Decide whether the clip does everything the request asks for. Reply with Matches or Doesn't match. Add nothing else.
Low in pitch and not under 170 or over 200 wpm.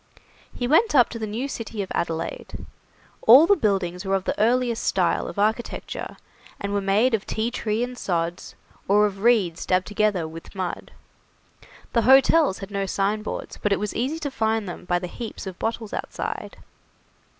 Doesn't match